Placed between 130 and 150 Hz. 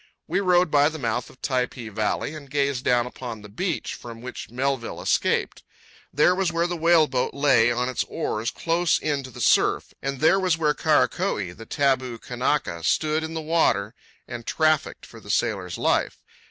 Yes: medium, 140 Hz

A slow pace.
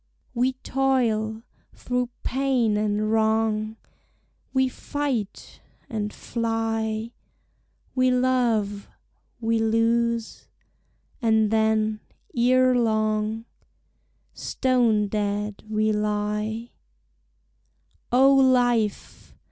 Yes: slow, 75 wpm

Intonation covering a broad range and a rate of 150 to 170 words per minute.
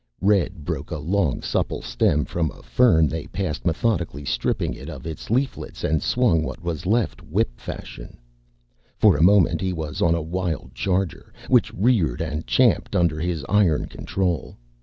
No: average, 3.8 semitones; average, 165 wpm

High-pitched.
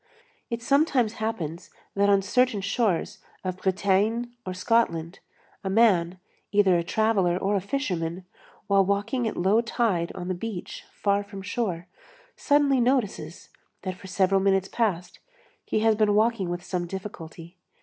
Yes: high, 200 Hz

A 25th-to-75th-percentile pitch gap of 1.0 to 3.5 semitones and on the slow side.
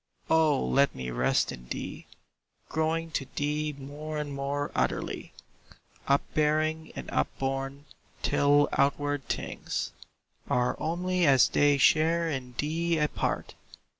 Yes: narrow, 2.4 semitones; slow, 120 wpm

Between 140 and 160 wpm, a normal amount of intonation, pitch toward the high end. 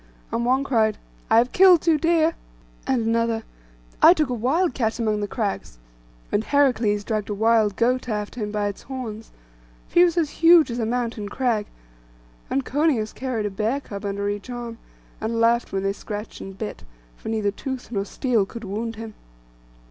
No: average, 185 wpm; average, 3.7 semitones; high, 230 Hz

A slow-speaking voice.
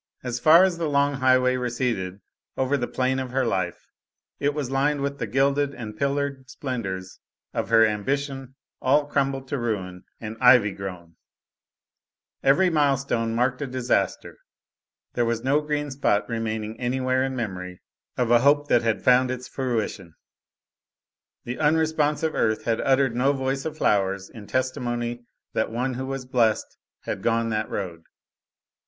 No: average, 155 wpm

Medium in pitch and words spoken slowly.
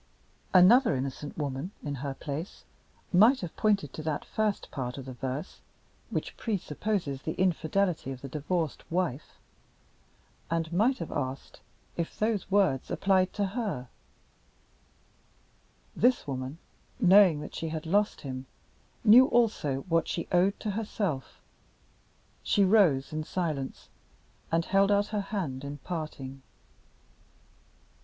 Yes: medium, 165 Hz; slow, 130 wpm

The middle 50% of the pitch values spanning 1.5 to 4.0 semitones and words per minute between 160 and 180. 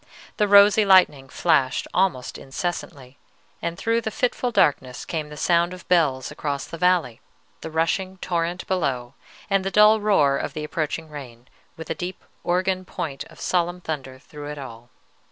No: average, 4.9 semitones; average, 165 wpm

